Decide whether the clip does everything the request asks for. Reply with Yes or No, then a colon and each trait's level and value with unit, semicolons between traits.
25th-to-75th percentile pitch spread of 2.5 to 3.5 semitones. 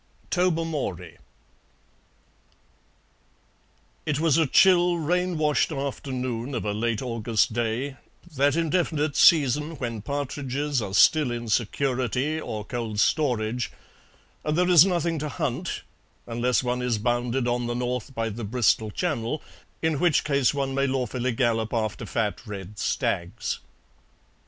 No: average, 4.5 semitones